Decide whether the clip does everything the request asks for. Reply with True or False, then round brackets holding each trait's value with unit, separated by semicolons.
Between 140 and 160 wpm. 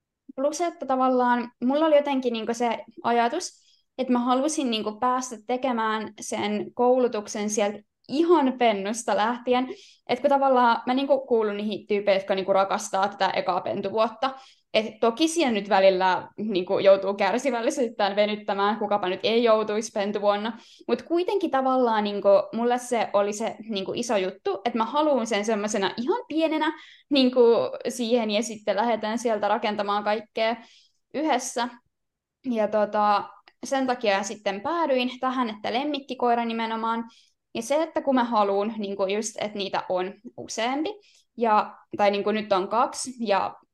True (150 wpm)